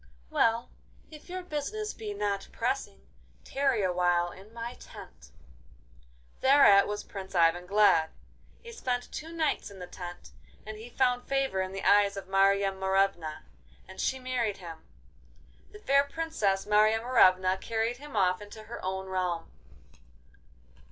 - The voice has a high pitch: Yes, high, 205 Hz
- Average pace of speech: Yes, average, 145 wpm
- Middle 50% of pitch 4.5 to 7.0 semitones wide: Yes, average, 5.0 semitones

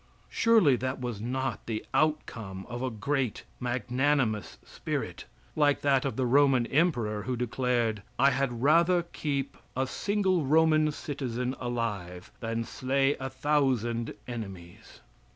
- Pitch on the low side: Yes, low, 130 Hz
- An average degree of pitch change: Yes, average, 3.7 semitones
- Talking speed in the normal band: No, slow, 130 wpm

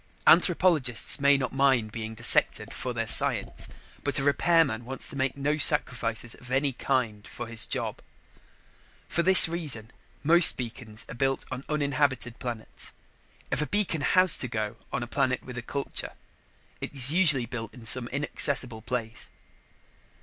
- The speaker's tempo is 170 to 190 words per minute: No, average, 155 wpm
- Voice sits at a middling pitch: No, low, 130 Hz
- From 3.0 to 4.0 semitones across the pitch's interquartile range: Yes, average, 3.6 semitones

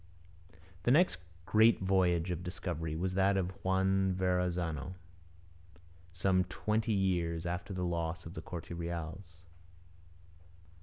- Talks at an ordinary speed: No, slow, 115 wpm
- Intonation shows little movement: Yes, narrow, 1.9 semitones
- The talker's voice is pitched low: Yes, very low, 90 Hz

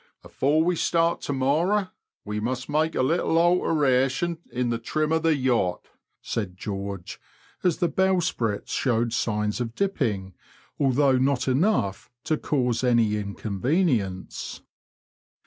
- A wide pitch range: Yes, wide, 6.4 semitones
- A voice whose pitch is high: No, low, 130 Hz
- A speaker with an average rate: No, slow, 130 wpm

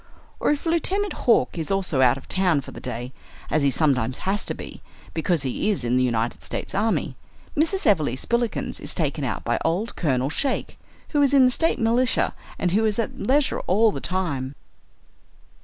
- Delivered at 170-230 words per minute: Yes, average, 190 wpm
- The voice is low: No, medium, 185 Hz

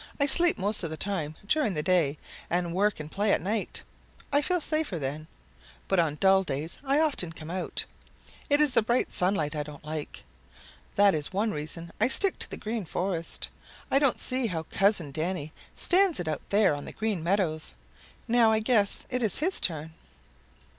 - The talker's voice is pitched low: No, high, 190 Hz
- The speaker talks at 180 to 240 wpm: Yes, average, 190 wpm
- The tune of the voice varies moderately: No, wide, 6.4 semitones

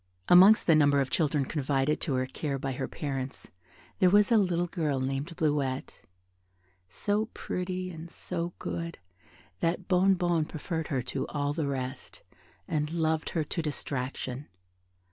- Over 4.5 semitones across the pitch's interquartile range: No, average, 4.2 semitones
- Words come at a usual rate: Yes, average, 145 wpm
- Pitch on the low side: No, medium, 155 Hz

